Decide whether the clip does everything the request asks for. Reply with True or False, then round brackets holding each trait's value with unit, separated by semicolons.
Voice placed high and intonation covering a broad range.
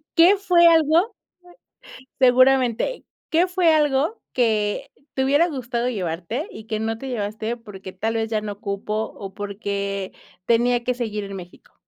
True (235 Hz; 5.7 semitones)